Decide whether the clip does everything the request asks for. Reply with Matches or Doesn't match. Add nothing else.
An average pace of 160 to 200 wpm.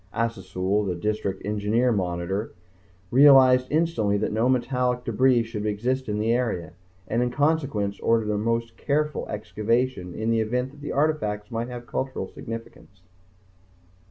Doesn't match